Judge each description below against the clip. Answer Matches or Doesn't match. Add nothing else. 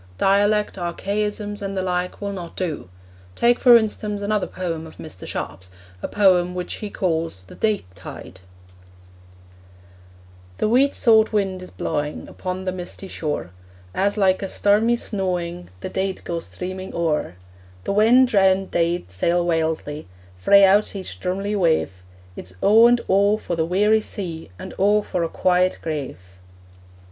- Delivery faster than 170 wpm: Doesn't match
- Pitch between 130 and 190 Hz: Matches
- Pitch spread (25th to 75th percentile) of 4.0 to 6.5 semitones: Doesn't match